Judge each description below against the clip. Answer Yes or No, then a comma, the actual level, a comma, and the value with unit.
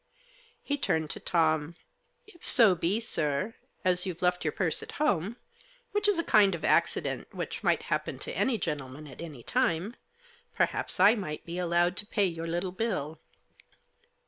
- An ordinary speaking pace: Yes, average, 170 wpm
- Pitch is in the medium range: Yes, medium, 180 Hz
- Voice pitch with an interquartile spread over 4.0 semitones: Yes, average, 4.5 semitones